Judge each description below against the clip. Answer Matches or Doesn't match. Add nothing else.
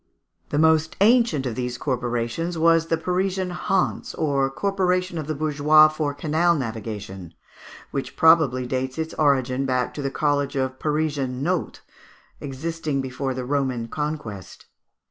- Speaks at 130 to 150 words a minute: Matches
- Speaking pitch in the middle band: Matches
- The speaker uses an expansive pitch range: Doesn't match